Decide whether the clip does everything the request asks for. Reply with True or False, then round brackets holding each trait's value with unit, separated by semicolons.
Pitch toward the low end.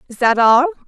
False (265 Hz)